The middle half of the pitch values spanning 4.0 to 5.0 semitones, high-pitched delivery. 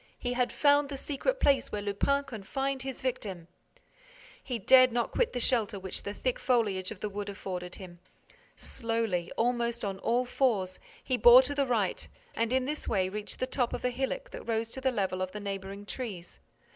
Yes: average, 4.7 semitones; high, 235 Hz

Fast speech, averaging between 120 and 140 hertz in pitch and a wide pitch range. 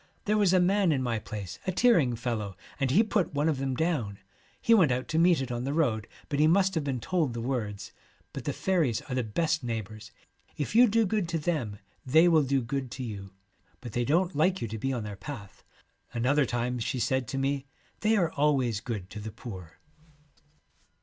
Yes: fast, 220 wpm; low, 135 Hz; wide, 6.1 semitones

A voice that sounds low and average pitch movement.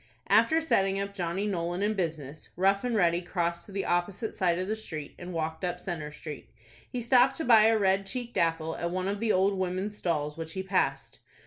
No: medium, 185 Hz; average, 3.3 semitones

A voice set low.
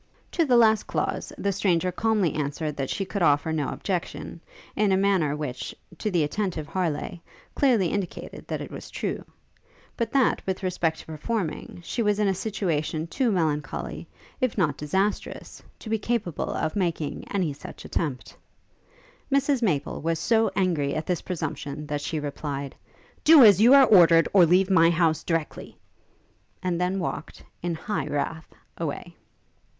No: medium, 175 Hz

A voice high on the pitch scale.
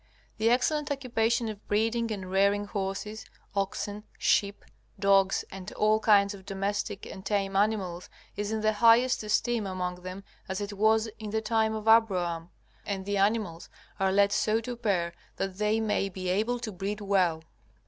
Yes: high, 205 Hz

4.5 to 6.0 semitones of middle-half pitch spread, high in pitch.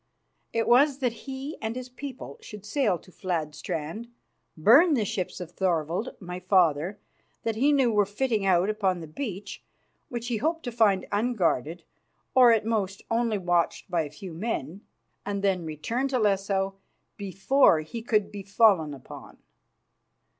Yes: average, 4.9 semitones; high, 205 Hz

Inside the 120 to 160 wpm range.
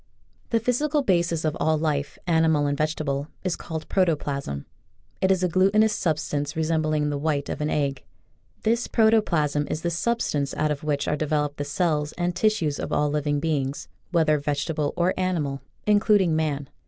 No: average, 170 wpm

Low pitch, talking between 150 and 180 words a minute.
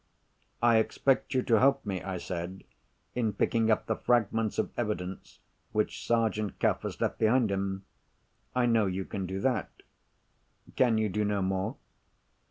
Yes: low, 110 Hz; average, 160 wpm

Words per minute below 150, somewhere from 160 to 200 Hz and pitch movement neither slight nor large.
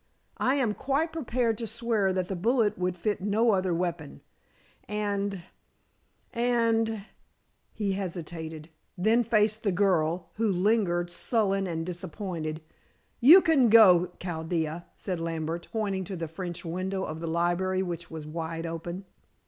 Yes: average, 140 wpm; medium, 185 Hz; average, 4.3 semitones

